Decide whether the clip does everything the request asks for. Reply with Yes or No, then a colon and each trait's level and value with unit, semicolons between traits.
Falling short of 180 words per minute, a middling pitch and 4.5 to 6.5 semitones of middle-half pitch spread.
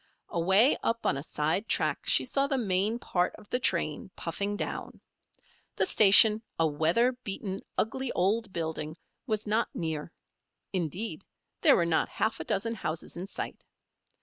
No: average, 155 wpm; high, 195 Hz; average, 5.1 semitones